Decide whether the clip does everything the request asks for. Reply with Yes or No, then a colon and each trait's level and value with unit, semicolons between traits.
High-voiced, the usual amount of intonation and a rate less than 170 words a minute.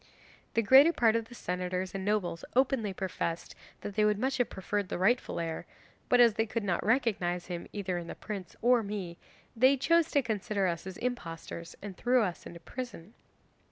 No: high, 205 Hz; average, 4.9 semitones; average, 190 wpm